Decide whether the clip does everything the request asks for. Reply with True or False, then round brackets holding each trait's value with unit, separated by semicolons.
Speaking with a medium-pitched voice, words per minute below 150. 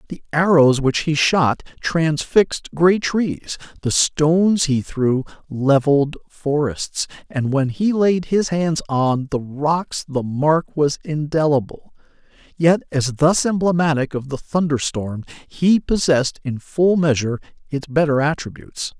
True (150 Hz; 135 wpm)